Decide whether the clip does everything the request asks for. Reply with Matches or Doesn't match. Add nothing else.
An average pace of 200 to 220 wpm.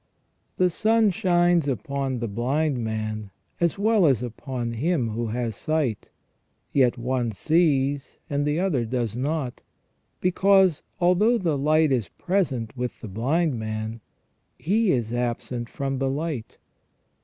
Doesn't match